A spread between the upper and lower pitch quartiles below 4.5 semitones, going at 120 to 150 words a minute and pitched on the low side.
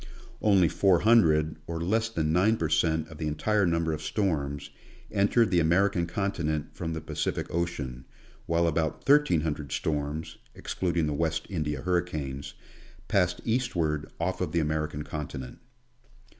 Yes: average, 3.0 semitones; average, 145 wpm; very low, 80 Hz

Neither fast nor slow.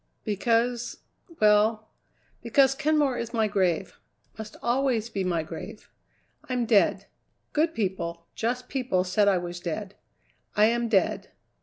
No: slow, 130 wpm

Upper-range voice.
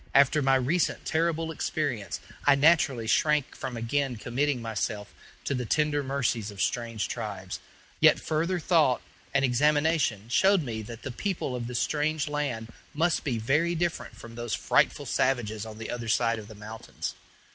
No: low, 130 Hz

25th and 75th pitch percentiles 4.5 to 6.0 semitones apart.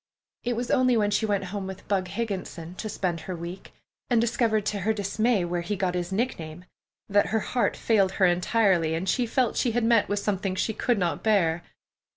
No: average, 3.8 semitones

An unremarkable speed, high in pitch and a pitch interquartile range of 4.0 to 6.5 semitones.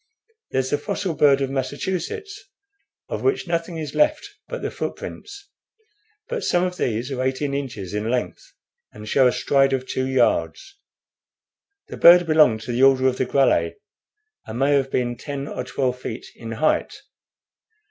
No: average, 165 wpm; low, 135 Hz; wide, 5.4 semitones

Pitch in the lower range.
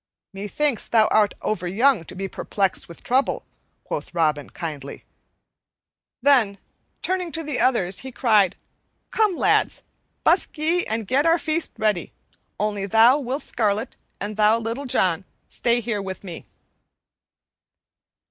No: high, 220 Hz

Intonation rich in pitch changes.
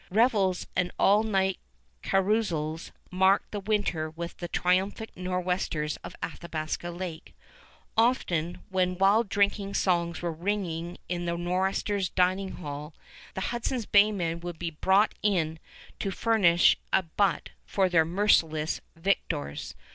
No: average, 2.8 semitones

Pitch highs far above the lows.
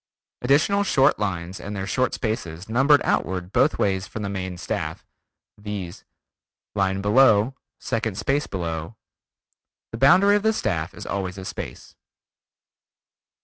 Yes: wide, 6.0 semitones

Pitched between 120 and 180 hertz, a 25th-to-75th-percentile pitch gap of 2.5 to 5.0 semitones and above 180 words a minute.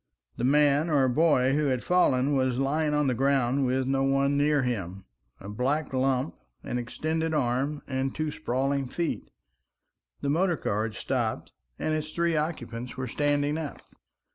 No: low, 135 Hz; average, 2.9 semitones; average, 165 wpm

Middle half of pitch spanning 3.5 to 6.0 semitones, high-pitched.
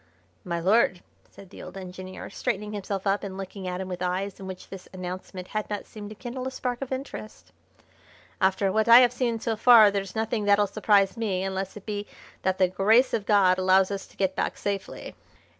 No: narrow, 2.4 semitones; high, 200 Hz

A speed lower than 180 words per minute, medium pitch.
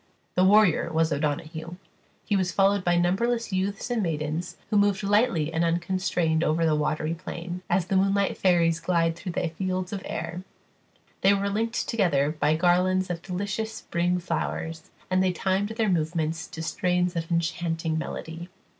Yes: average, 165 wpm; medium, 175 Hz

